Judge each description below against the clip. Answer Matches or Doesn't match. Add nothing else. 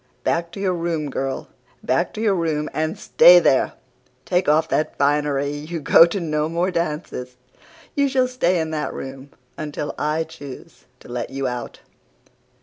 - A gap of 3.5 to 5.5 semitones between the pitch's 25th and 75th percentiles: Doesn't match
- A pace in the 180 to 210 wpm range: Doesn't match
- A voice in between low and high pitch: Matches